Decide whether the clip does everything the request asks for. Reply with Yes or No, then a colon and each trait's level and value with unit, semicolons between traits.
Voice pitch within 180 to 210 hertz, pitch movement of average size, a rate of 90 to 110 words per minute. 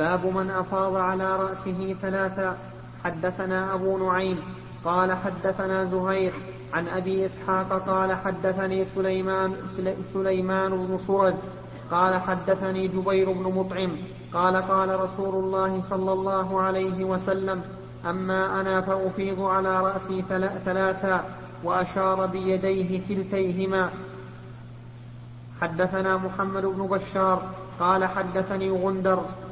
No: high, 190 Hz; narrow, 0.5 semitones; average, 100 wpm